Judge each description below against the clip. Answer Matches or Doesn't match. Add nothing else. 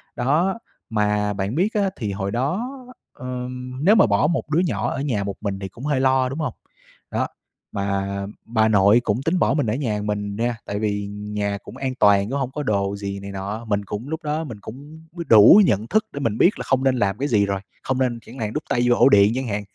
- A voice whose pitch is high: Doesn't match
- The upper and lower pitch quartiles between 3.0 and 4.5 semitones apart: Doesn't match